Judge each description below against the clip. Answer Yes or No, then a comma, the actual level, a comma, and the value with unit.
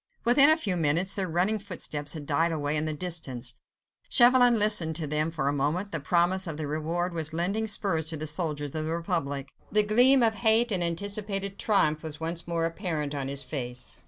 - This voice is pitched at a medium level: Yes, medium, 165 Hz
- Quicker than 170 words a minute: Yes, fast, 205 wpm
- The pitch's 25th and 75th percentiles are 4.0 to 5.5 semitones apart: Yes, average, 4.8 semitones